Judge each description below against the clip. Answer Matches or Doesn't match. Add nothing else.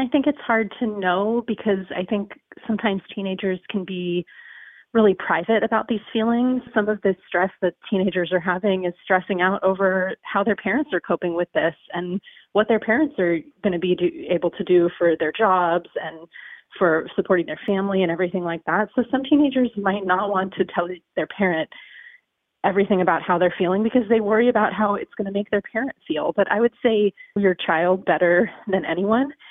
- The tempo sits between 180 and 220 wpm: Matches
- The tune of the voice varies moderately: Matches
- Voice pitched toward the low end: Doesn't match